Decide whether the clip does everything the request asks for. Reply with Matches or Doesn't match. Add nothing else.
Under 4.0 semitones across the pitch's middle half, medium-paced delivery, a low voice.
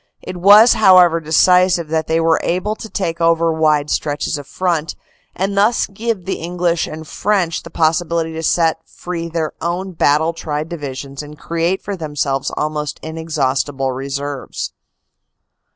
Doesn't match